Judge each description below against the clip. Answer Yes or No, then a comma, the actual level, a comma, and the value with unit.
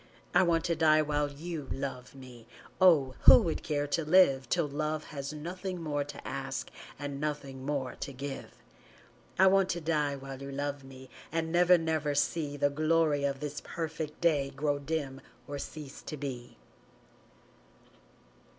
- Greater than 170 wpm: No, average, 160 wpm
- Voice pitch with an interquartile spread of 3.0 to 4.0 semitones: No, narrow, 2.6 semitones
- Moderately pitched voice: Yes, medium, 145 Hz